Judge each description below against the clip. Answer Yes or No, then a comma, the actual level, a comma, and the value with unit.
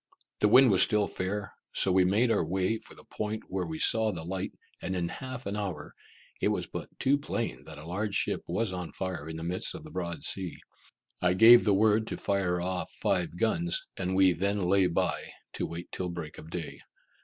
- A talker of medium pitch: No, very low, 95 Hz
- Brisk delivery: Yes, fast, 215 wpm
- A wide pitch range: No, average, 3.2 semitones